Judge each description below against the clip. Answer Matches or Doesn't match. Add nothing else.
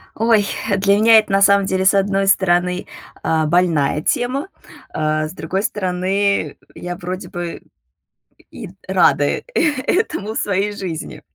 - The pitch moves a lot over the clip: Doesn't match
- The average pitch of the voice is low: Doesn't match